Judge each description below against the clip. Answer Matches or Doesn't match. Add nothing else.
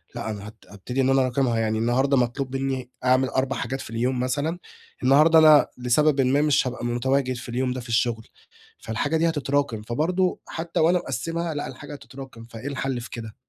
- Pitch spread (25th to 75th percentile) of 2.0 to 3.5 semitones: Matches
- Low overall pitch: Matches